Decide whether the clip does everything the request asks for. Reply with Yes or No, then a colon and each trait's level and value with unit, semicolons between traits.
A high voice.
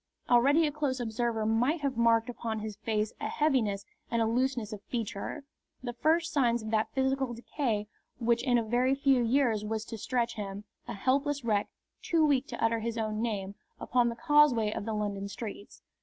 Yes: high, 235 Hz